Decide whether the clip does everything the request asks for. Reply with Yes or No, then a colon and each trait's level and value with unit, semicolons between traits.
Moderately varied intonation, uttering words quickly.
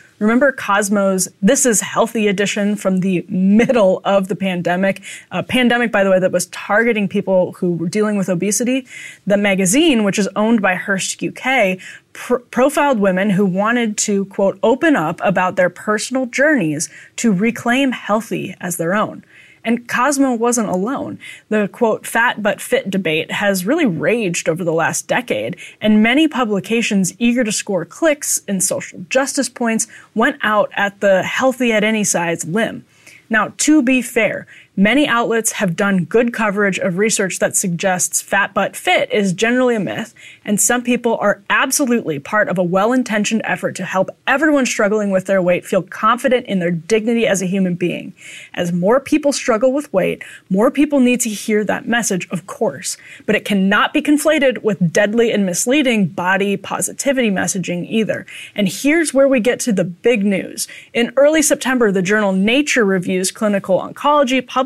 No: average, 4.4 semitones; average, 170 wpm